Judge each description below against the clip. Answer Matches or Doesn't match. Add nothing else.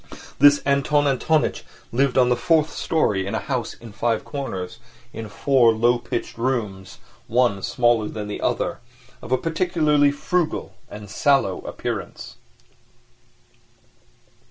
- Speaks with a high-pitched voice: Doesn't match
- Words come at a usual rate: Doesn't match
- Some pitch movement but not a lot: Matches